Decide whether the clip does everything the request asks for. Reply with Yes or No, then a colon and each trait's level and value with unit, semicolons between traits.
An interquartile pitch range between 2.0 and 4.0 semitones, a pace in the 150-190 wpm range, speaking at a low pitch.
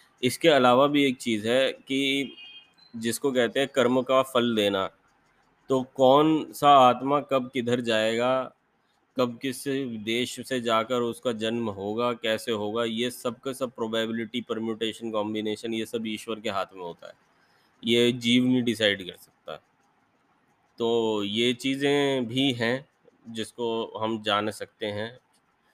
No: narrow, 2.5 semitones; average, 140 wpm; low, 120 Hz